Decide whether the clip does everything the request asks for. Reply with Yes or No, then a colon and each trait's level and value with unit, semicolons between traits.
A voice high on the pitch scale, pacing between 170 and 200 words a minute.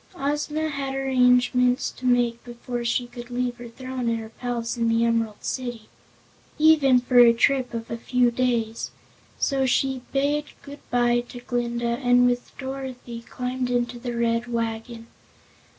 No: high, 245 Hz; average, 155 wpm